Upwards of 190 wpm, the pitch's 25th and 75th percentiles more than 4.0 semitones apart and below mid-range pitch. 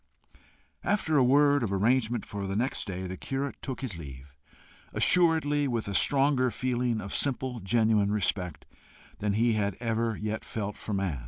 No: average, 160 wpm; average, 4.7 semitones; low, 115 Hz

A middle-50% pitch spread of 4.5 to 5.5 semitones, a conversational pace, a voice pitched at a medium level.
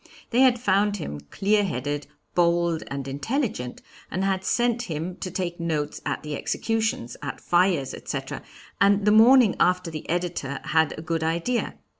Yes: average, 4.9 semitones; average, 160 wpm; medium, 175 Hz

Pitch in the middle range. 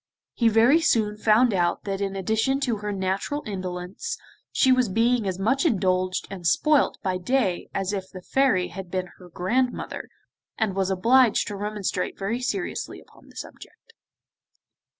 No: high, 205 Hz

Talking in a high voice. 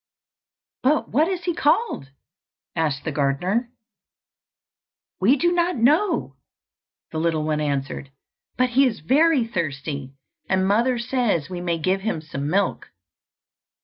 Yes: high, 195 Hz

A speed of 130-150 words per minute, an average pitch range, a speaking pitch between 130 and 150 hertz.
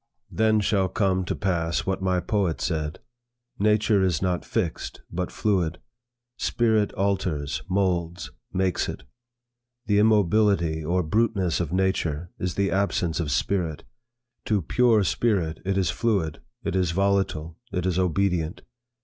No: slow, 135 wpm; average, 3.0 semitones; very low, 95 Hz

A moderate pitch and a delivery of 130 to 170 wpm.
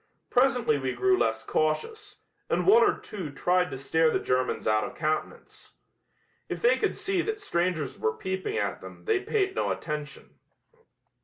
Yes: medium, 180 Hz; average, 165 wpm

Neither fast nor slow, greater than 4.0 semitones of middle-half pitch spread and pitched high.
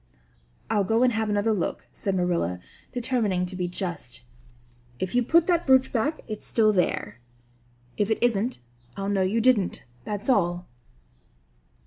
Yes: average, 150 wpm; average, 4.6 semitones; high, 205 Hz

